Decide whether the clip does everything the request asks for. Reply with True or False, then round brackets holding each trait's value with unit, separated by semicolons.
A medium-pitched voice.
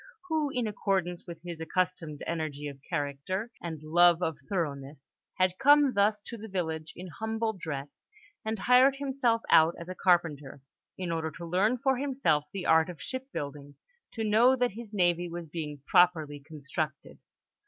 True (175 Hz)